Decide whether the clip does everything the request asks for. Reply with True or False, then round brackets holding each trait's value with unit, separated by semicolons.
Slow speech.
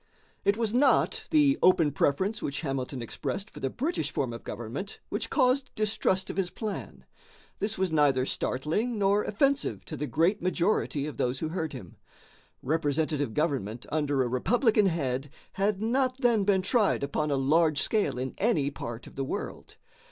False (170 wpm)